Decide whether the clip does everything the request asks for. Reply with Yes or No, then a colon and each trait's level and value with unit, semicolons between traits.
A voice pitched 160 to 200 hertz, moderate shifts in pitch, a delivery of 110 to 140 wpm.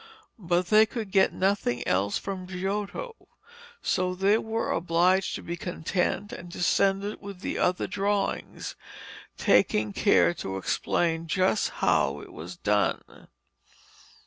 Yes: medium, 185 Hz; average, 3.4 semitones; slow, 135 wpm